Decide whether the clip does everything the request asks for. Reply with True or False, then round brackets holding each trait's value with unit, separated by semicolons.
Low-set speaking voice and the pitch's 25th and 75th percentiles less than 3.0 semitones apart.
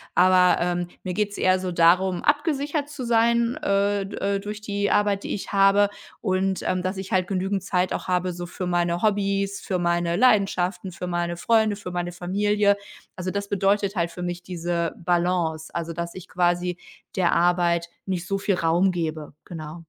False (185 Hz; 2.5 semitones)